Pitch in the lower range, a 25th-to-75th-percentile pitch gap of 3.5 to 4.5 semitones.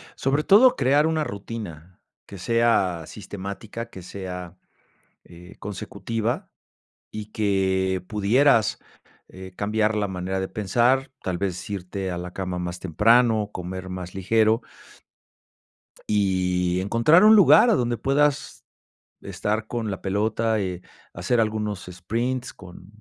Yes: low, 100 Hz; average, 3.9 semitones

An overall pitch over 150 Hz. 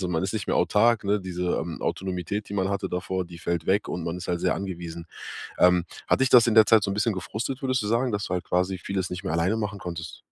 No: very low, 95 Hz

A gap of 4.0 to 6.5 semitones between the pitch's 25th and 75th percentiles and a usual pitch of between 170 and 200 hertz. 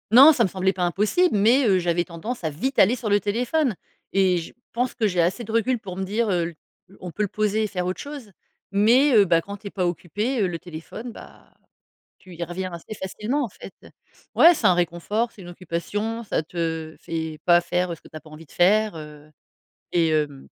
Yes: average, 4.5 semitones; high, 190 Hz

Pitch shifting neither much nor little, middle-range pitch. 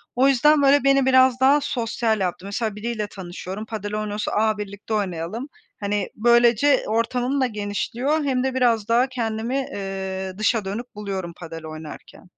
No: average, 4.0 semitones; high, 220 Hz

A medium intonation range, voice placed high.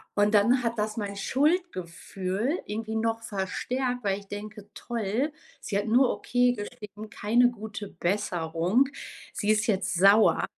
Yes: average, 3.1 semitones; high, 215 Hz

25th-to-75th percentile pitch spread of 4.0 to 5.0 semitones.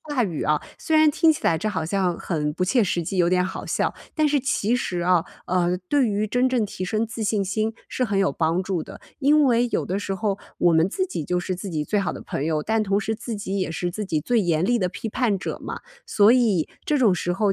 Yes: average, 4.7 semitones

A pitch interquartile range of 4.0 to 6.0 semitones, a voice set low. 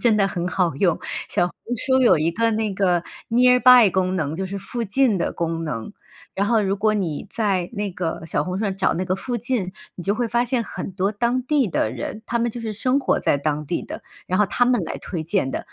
No: average, 5.0 semitones; high, 200 Hz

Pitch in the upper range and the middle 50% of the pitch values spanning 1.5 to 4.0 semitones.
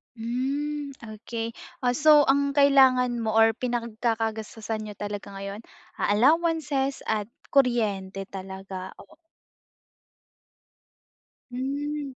No: high, 235 Hz; average, 4.6 semitones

